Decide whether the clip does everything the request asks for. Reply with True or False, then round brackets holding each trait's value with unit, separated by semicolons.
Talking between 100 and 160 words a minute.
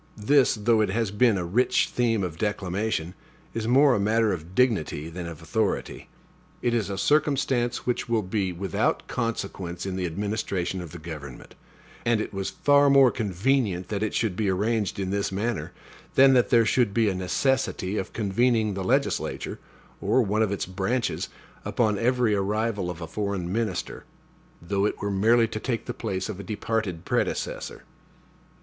False (175 wpm)